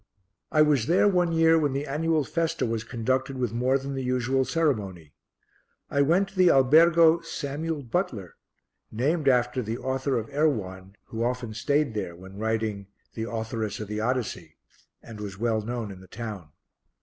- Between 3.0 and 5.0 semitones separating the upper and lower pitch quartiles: No, wide, 5.5 semitones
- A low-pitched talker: Yes, low, 125 Hz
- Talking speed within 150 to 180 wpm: Yes, average, 170 wpm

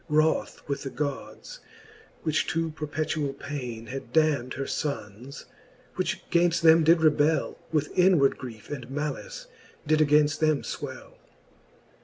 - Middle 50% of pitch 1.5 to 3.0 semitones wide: Yes, narrow, 2.5 semitones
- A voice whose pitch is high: No, medium, 150 Hz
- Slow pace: Yes, slow, 130 wpm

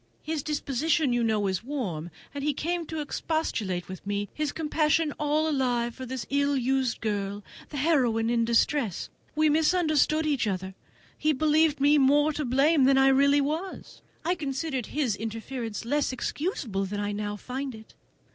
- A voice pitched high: Yes, very high, 270 Hz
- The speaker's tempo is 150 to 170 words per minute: Yes, average, 165 wpm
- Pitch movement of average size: Yes, average, 5.0 semitones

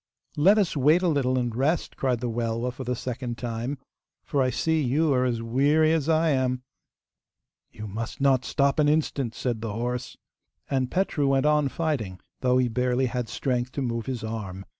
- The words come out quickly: No, average, 190 wpm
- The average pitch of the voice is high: No, low, 130 Hz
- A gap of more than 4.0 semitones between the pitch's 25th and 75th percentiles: No, average, 3.5 semitones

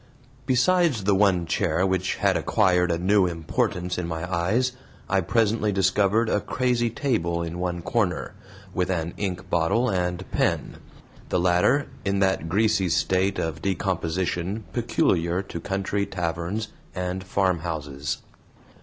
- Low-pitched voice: Yes, very low, 95 Hz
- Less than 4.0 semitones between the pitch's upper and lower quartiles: Yes, average, 3.1 semitones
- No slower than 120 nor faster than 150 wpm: Yes, slow, 135 wpm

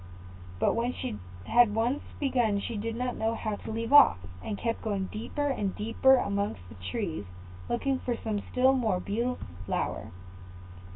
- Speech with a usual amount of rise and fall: Yes, average, 3.4 semitones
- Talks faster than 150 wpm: Yes, average, 165 wpm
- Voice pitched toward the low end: No, high, 230 Hz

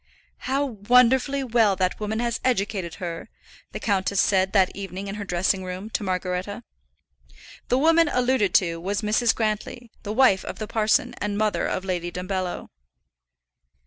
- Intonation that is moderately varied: Yes, average, 4.0 semitones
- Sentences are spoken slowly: No, average, 155 wpm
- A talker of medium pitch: No, high, 205 Hz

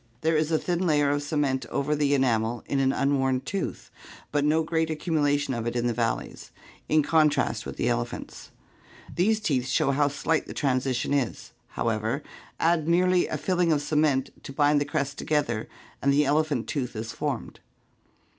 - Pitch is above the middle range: No, medium, 145 Hz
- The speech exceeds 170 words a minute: Yes, average, 180 wpm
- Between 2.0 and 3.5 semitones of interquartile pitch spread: Yes, average, 2.8 semitones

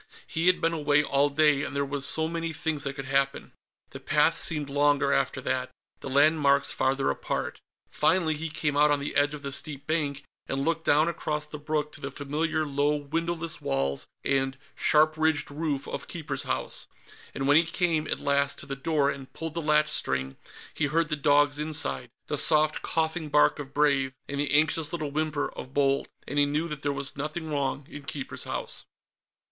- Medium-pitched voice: Yes, medium, 145 Hz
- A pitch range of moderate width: No, narrow, 1.9 semitones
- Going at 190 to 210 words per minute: Yes, average, 195 wpm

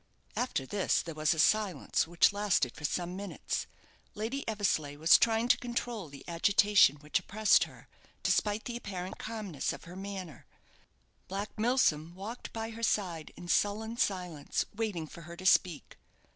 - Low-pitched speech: No, high, 195 Hz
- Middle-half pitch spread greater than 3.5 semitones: Yes, average, 4.5 semitones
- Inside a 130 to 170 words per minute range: Yes, average, 160 wpm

